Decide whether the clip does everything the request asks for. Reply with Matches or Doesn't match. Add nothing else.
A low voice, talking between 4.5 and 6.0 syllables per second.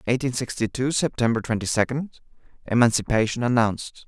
Matches